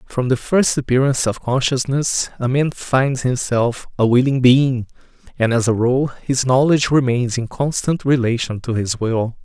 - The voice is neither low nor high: No, low, 125 Hz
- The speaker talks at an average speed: Yes, average, 165 wpm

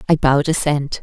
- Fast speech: No, average, 175 wpm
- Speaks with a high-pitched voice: No, medium, 145 Hz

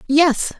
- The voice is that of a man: No, female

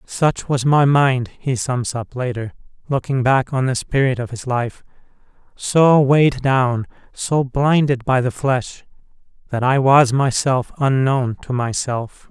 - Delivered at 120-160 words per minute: Yes, average, 150 wpm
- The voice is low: Yes, low, 130 Hz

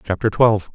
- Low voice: Yes, low, 105 Hz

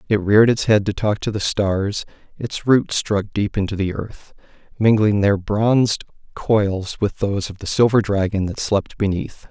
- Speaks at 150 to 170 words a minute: No, average, 185 wpm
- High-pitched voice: No, low, 105 Hz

